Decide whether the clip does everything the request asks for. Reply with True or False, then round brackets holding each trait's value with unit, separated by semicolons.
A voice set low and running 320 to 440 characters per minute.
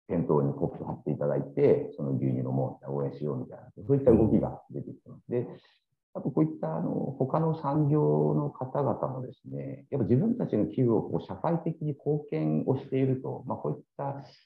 True (80 Hz; 405 characters per minute)